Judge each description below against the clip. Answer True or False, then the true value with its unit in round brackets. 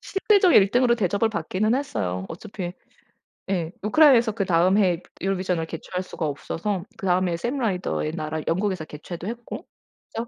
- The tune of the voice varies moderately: True (4.9 semitones)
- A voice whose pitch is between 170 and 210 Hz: True (190 Hz)